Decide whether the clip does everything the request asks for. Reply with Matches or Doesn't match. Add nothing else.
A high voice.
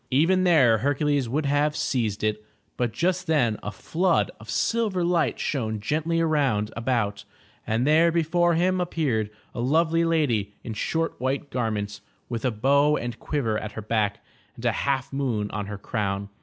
Doesn't match